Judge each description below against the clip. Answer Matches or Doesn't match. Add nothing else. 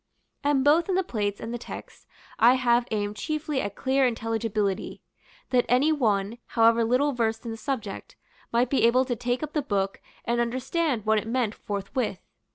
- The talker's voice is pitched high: Matches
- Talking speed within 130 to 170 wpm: Doesn't match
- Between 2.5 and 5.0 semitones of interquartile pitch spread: Matches